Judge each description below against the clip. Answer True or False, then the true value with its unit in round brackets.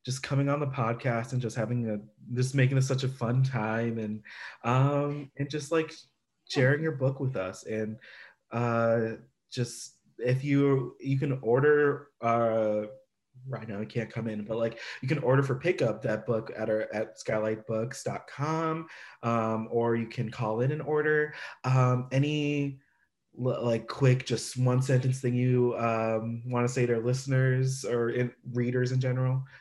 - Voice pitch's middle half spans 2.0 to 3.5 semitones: True (2.8 semitones)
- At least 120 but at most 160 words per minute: False (170 wpm)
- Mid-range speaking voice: False (125 Hz)